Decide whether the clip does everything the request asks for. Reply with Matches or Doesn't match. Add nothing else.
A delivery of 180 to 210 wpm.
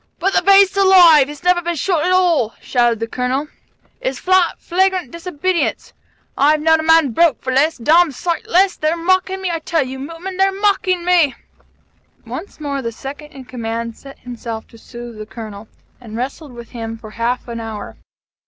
Matches